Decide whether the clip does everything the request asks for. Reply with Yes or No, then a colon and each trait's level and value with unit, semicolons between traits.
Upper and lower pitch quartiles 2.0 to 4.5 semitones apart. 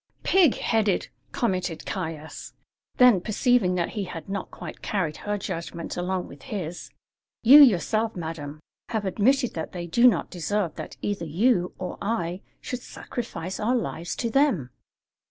No: average, 5.1 semitones